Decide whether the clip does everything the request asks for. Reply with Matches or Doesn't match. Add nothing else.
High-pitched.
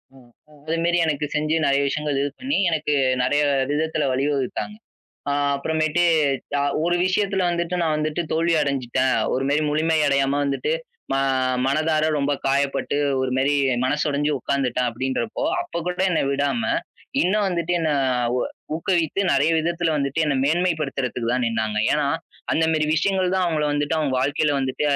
Doesn't match